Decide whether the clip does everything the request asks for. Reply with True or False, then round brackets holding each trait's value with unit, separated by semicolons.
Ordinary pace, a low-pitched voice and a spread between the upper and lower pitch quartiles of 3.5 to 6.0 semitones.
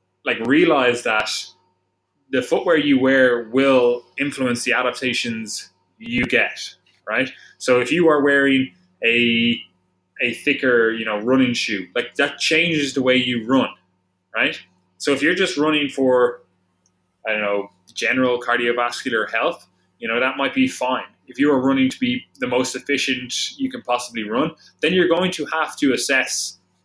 True (160 wpm; 125 Hz; 5.0 semitones)